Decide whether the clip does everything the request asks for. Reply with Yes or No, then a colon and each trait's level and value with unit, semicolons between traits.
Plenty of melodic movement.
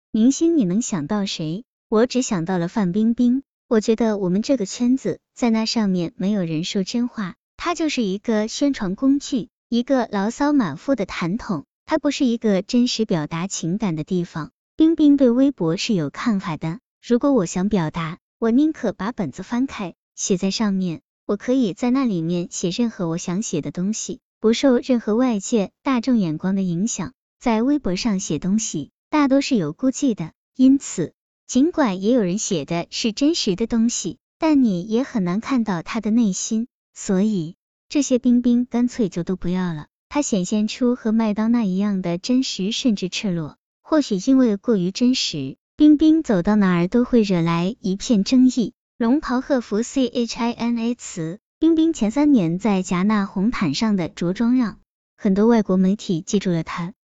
No: average, 5.0 semitones